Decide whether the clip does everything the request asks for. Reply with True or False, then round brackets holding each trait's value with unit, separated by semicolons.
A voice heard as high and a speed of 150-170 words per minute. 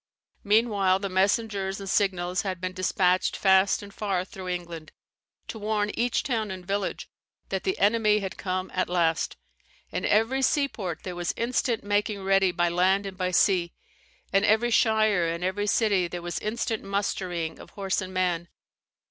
True (195 Hz; 165 wpm)